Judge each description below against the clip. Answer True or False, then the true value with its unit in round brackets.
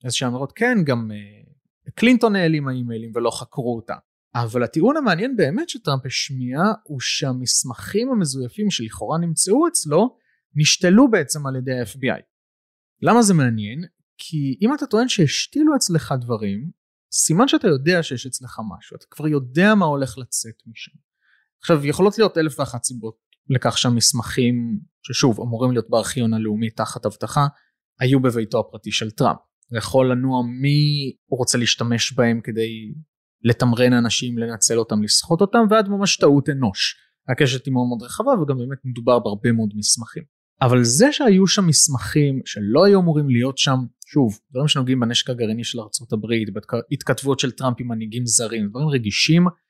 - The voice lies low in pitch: True (130 Hz)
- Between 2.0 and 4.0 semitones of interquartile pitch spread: False (5.4 semitones)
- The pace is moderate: False (155 wpm)